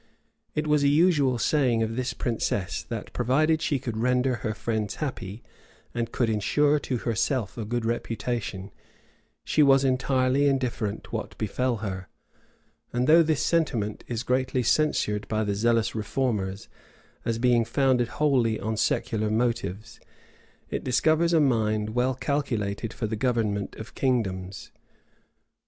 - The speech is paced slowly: No, average, 145 wpm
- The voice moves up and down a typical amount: Yes, average, 3.6 semitones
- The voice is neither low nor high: No, low, 120 Hz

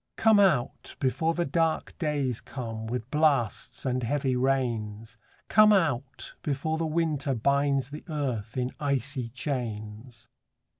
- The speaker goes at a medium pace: No, slow, 130 wpm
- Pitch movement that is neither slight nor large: Yes, average, 4.0 semitones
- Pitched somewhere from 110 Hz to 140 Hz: Yes, low, 135 Hz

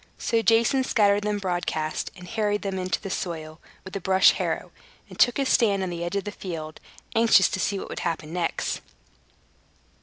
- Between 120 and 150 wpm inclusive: No, average, 190 wpm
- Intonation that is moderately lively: Yes, average, 3.2 semitones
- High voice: Yes, high, 195 Hz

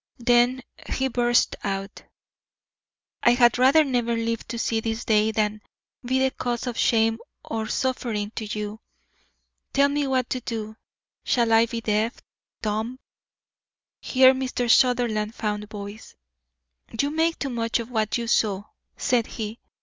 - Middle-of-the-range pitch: No, high, 230 Hz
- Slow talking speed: No, average, 150 wpm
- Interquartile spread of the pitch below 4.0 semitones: Yes, narrow, 2.5 semitones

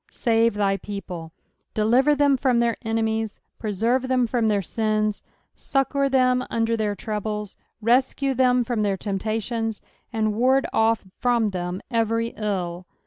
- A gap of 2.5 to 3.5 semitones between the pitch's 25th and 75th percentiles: Yes, average, 2.9 semitones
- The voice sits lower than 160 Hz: No, high, 225 Hz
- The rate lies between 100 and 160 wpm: Yes, average, 140 wpm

